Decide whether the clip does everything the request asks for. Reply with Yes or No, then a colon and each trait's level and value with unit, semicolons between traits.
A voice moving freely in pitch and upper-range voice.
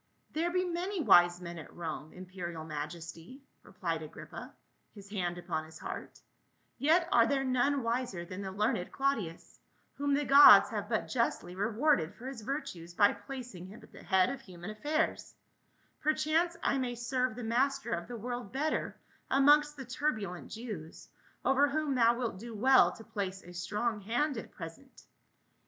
Yes: wide, 7.2 semitones; high, 230 Hz